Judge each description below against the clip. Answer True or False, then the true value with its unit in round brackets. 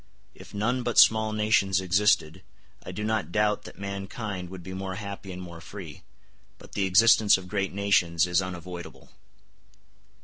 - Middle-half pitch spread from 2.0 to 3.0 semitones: True (2.5 semitones)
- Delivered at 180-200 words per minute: False (160 wpm)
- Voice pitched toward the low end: True (95 Hz)